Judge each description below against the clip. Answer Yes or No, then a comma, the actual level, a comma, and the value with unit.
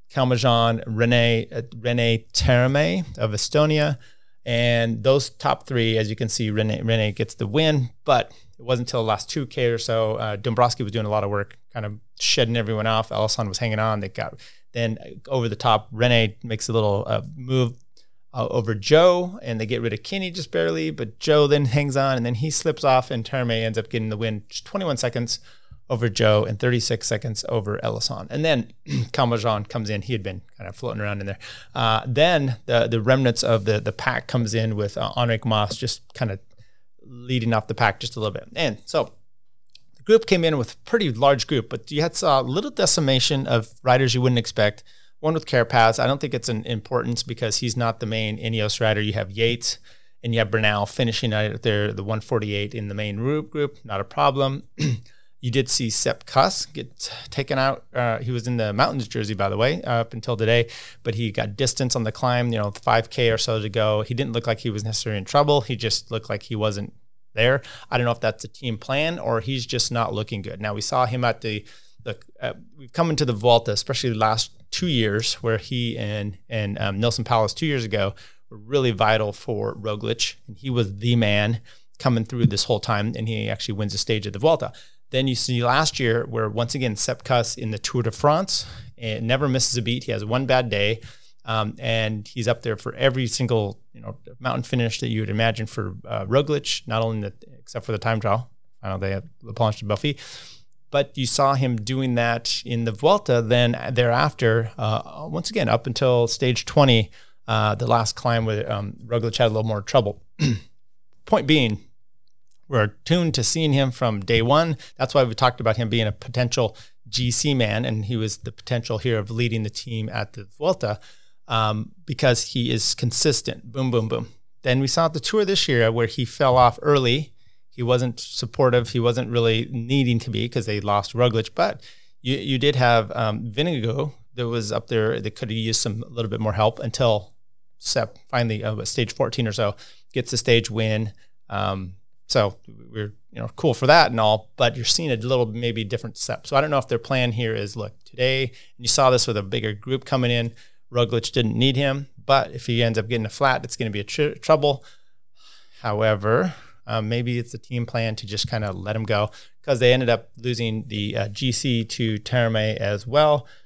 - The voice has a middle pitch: No, low, 115 Hz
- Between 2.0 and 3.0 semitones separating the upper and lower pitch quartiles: Yes, narrow, 2.5 semitones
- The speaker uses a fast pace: Yes, fast, 215 wpm